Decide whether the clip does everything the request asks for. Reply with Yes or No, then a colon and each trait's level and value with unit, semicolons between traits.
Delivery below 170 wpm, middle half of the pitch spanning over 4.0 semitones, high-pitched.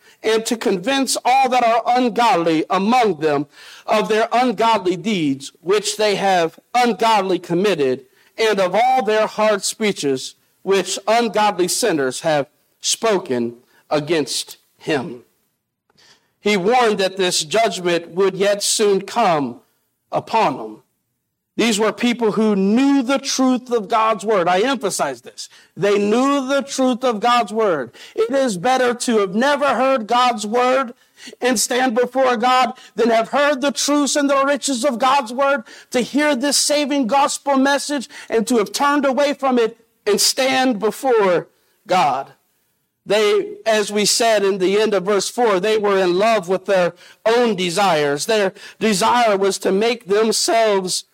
Yes: average, 150 wpm; average, 4.7 semitones; high, 225 Hz